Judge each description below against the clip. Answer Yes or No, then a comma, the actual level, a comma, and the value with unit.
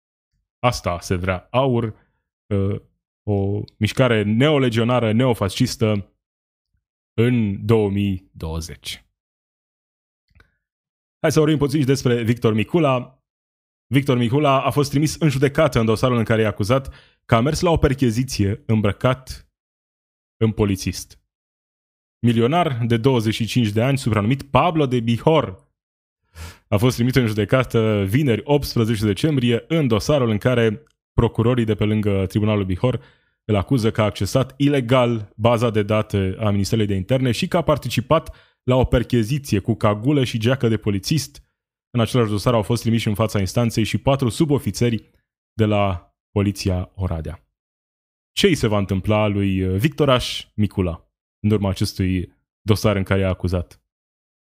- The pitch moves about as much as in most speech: Yes, average, 4.3 semitones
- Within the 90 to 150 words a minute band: Yes, average, 140 wpm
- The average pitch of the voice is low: Yes, low, 110 Hz